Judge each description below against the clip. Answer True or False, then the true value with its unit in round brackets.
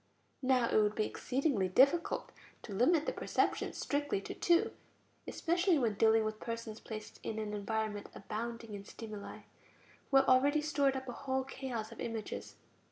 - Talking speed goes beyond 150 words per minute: True (165 wpm)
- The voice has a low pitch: False (230 Hz)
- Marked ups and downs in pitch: False (4.0 semitones)